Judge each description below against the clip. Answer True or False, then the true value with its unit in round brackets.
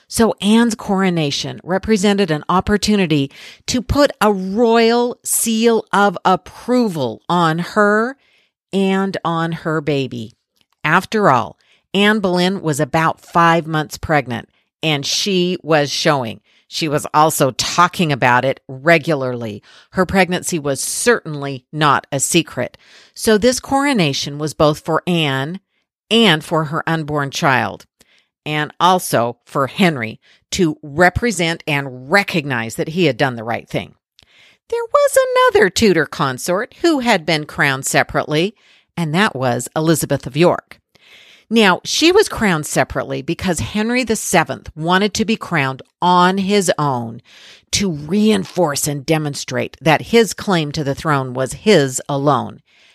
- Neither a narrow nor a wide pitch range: False (5.8 semitones)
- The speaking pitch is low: False (165 Hz)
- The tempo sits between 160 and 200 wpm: False (135 wpm)